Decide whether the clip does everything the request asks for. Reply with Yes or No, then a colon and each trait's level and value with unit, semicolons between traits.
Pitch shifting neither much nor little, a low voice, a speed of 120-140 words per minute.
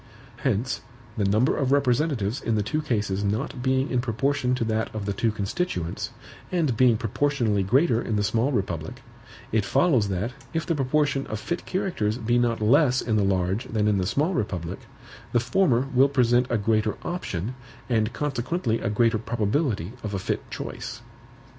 No: average, 4.6 semitones; low, 115 Hz; average, 175 wpm